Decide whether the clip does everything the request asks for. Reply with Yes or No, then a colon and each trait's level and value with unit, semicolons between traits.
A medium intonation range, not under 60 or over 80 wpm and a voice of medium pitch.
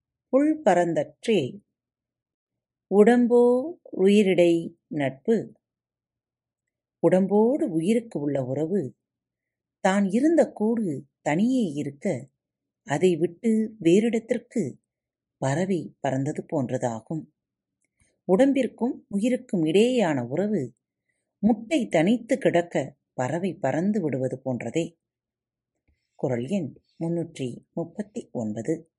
No: wide, 8.7 semitones; slow, 75 wpm; medium, 170 Hz